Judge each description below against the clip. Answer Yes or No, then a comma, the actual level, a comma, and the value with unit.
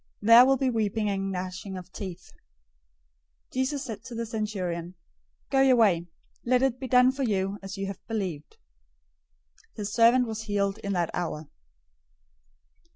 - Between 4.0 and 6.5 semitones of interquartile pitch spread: Yes, average, 4.3 semitones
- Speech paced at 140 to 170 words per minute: Yes, average, 155 wpm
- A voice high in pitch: Yes, high, 210 Hz